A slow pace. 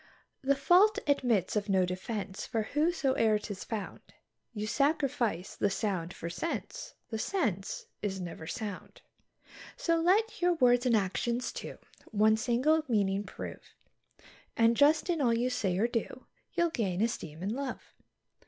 No: average, 145 wpm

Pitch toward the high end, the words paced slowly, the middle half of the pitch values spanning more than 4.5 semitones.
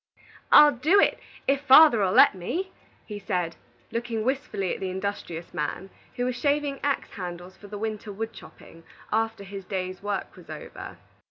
No: high, 210 Hz; average, 165 wpm; average, 5.3 semitones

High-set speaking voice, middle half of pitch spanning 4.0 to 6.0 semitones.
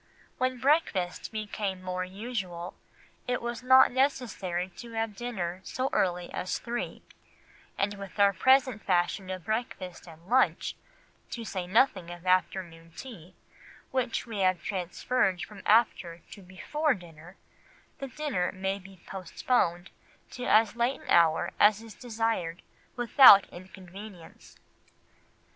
Yes: high, 195 Hz; average, 4.9 semitones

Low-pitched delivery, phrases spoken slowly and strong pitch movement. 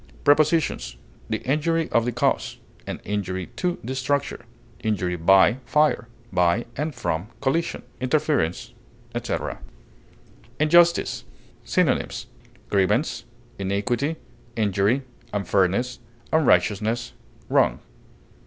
Yes: low, 120 Hz; slow, 90 wpm; wide, 7.1 semitones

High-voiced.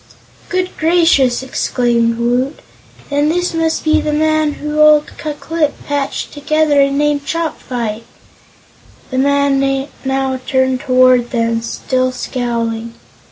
Yes: very high, 275 Hz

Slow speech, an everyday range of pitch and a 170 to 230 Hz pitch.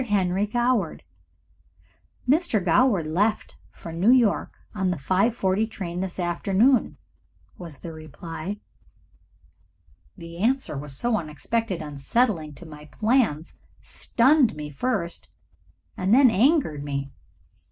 No: slow, 115 wpm; wide, 6.4 semitones; high, 190 Hz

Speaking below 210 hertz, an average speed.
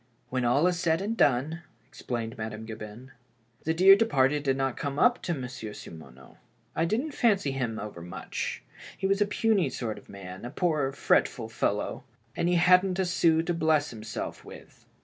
Yes: low, 135 Hz; average, 190 wpm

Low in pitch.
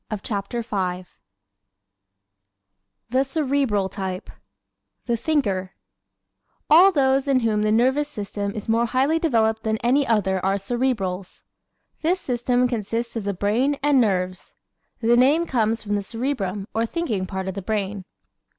No: high, 225 Hz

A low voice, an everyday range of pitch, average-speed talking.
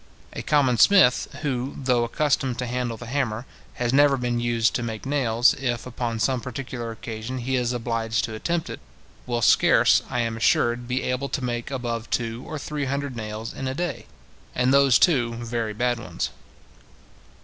No: low, 125 Hz; narrow, 2.3 semitones; average, 180 wpm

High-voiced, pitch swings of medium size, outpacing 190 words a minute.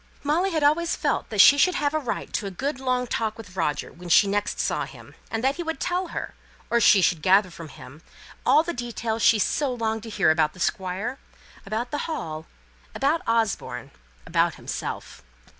No: high, 230 Hz; wide, 7.2 semitones; average, 200 wpm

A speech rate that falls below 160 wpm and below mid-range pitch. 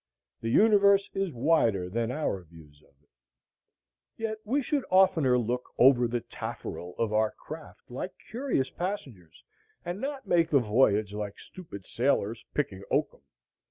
Yes: average, 145 wpm; low, 125 Hz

